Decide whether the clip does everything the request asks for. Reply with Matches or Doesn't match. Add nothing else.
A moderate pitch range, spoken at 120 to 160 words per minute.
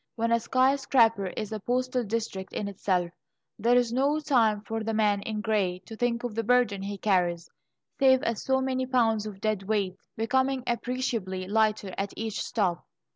Doesn't match